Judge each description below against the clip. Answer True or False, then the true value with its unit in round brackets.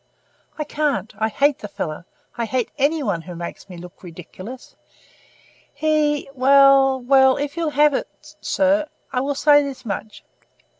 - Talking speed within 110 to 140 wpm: False (155 wpm)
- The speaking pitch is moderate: False (270 Hz)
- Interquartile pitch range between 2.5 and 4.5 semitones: False (5.1 semitones)